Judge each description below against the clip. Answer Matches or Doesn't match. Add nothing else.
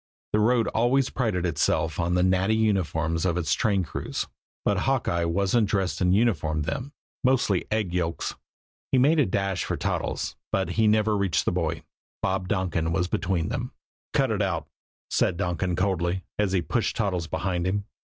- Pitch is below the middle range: Matches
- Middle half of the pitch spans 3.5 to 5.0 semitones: Matches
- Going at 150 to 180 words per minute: Matches